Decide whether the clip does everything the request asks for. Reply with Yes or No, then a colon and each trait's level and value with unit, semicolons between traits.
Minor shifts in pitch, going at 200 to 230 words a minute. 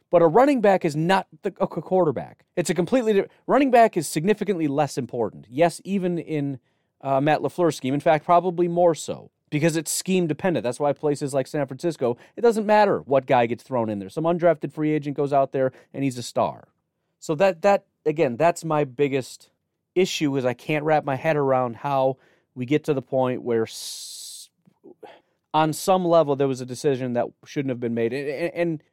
No: average, 4.2 semitones; fast, 205 wpm